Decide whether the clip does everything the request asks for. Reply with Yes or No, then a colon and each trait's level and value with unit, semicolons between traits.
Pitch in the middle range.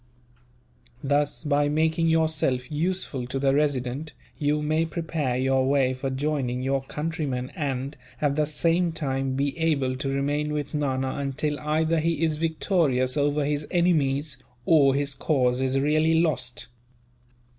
Yes: medium, 145 Hz